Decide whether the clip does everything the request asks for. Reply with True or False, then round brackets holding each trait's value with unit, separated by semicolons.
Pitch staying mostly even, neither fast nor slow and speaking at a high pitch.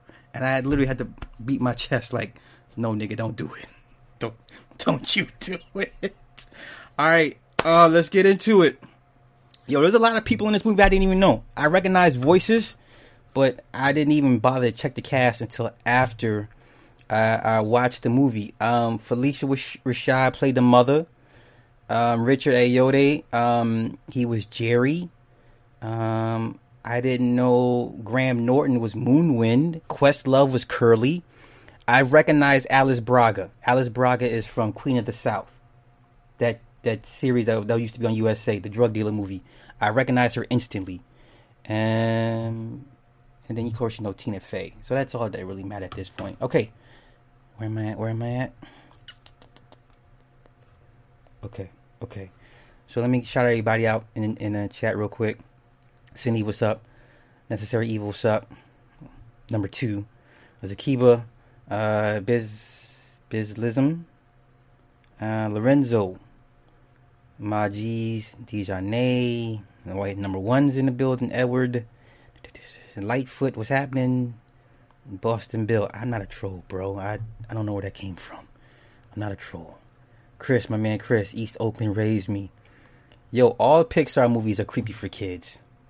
False (2.1 semitones; 155 wpm; 120 Hz)